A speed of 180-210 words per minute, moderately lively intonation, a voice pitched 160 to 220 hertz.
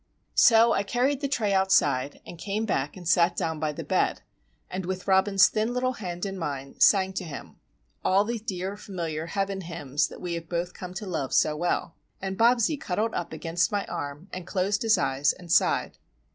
Yes: average, 195 wpm; average, 3.7 semitones; medium, 185 Hz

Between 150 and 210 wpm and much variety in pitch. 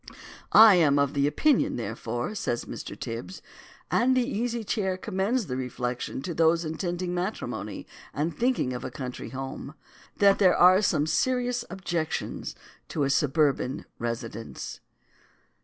No: slow, 135 wpm; wide, 7.7 semitones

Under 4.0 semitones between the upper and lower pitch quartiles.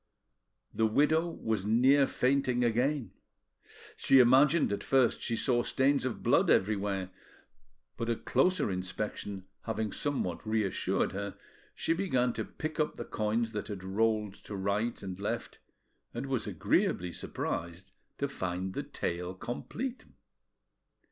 No: average, 5.1 semitones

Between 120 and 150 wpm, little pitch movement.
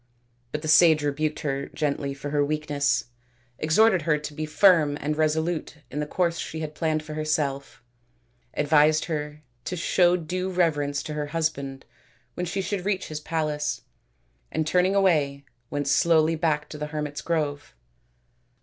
No: average, 160 wpm; narrow, 2.0 semitones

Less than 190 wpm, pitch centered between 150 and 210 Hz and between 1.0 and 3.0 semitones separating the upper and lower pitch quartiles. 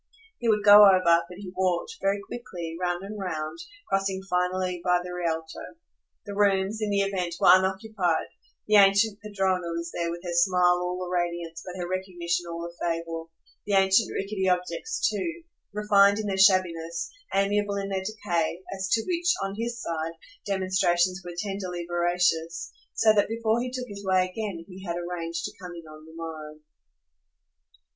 Yes: average, 175 wpm; medium, 185 Hz; average, 2.7 semitones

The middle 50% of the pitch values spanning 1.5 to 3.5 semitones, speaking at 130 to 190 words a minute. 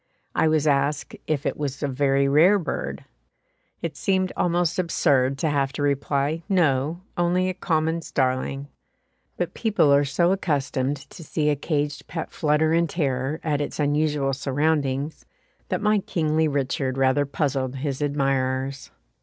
Yes: average, 2.8 semitones; average, 150 wpm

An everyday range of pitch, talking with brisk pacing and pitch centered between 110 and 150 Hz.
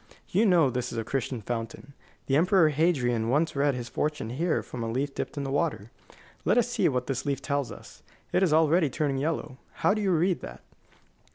Yes: average, 4.5 semitones; fast, 210 wpm; medium, 140 Hz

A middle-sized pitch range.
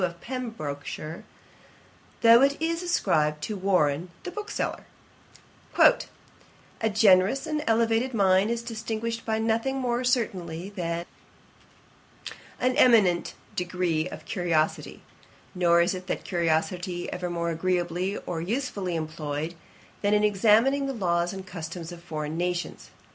Yes: average, 5.0 semitones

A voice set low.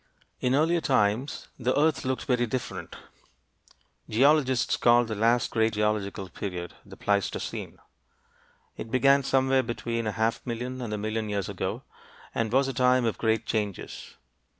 Yes: low, 120 Hz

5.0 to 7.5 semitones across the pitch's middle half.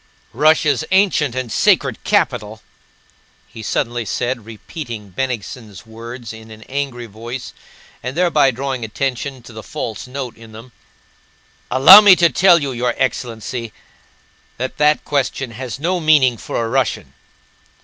No: average, 3.6 semitones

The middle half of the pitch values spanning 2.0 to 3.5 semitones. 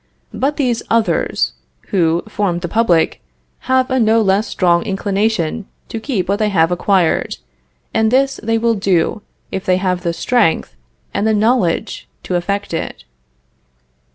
No: average, 4.2 semitones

